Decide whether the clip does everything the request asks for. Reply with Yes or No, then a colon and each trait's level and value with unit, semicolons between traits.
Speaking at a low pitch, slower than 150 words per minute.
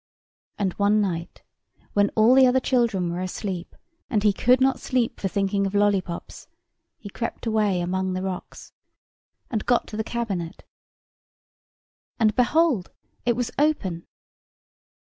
No: high, 205 Hz; average, 140 wpm